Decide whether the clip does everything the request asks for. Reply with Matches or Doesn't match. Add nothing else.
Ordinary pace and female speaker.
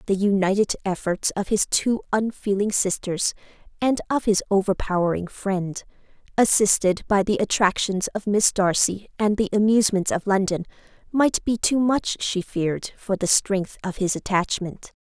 Matches